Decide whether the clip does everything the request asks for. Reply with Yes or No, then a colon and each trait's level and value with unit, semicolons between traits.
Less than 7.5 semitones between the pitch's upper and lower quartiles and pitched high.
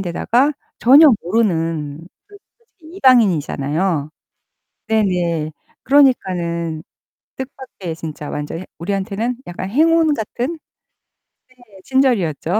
No: wide, 8.1 semitones; high, 195 Hz